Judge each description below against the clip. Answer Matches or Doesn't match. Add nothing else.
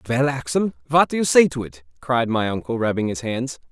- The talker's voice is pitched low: Matches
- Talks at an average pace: Doesn't match